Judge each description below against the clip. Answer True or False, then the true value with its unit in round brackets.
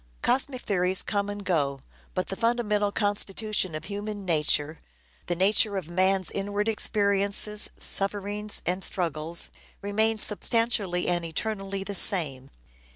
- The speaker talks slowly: True (125 wpm)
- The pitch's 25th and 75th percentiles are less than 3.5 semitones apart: True (2.8 semitones)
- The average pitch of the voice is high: True (200 Hz)